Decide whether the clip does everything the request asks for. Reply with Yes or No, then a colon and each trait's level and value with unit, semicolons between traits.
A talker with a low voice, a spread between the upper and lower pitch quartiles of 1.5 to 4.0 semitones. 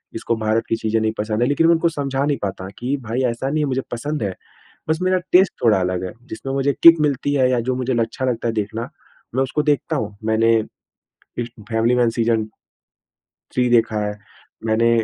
Yes: low, 120 Hz; average, 3.7 semitones